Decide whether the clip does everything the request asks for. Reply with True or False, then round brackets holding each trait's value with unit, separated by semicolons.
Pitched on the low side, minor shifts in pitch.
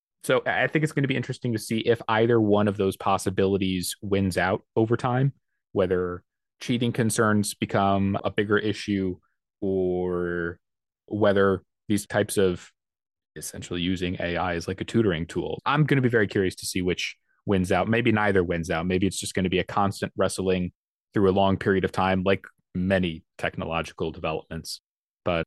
False (100 Hz; 3.1 semitones)